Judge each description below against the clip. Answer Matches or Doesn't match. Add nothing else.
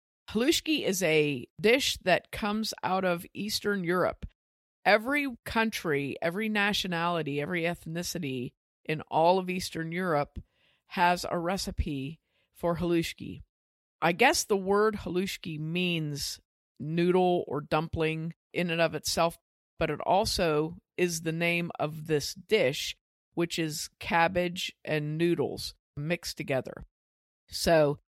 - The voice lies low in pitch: Doesn't match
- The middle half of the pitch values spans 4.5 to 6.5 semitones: Doesn't match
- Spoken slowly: Matches